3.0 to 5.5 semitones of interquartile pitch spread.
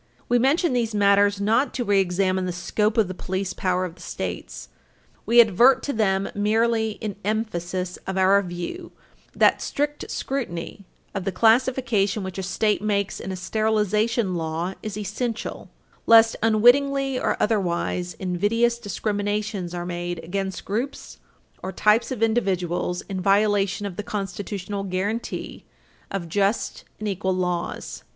Yes: average, 3.3 semitones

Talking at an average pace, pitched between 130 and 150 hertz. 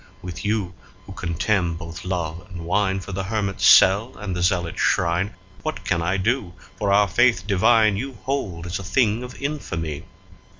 No: average, 170 wpm; very low, 95 Hz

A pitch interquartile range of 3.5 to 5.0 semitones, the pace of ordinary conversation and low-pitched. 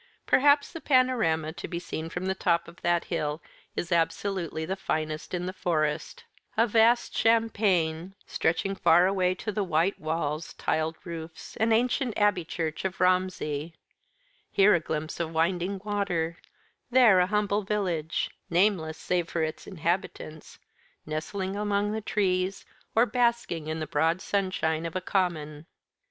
No: average, 3.9 semitones; average, 150 wpm; medium, 180 Hz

